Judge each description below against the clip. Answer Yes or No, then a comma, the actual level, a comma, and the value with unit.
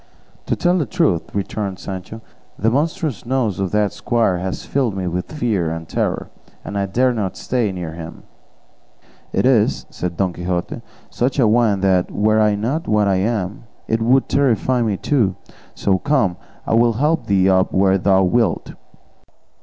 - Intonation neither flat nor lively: Yes, average, 4.4 semitones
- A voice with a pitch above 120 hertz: No, low, 105 Hz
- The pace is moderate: Yes, average, 170 wpm